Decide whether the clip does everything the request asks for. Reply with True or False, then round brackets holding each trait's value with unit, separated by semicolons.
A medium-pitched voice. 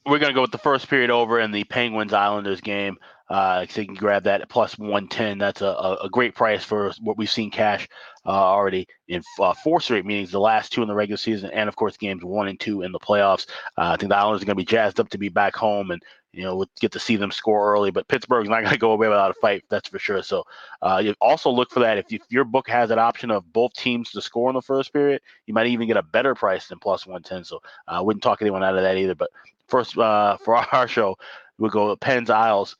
False (105 Hz)